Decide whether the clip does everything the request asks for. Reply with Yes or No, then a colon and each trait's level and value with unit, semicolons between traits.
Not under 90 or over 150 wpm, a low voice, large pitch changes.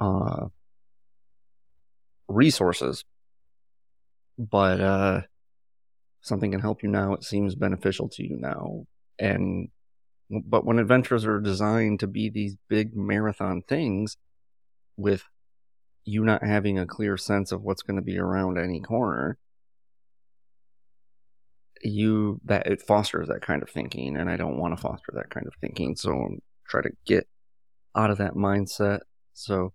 No: average, 140 wpm; very low, 95 Hz; average, 3.0 semitones